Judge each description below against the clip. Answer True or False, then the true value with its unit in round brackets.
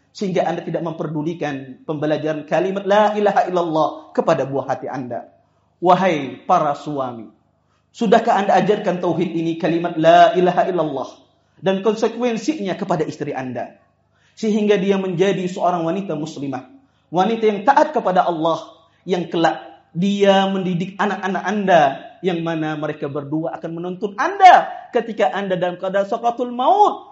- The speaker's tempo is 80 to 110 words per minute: False (135 wpm)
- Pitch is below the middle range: False (180 Hz)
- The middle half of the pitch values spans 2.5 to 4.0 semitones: False (4.7 semitones)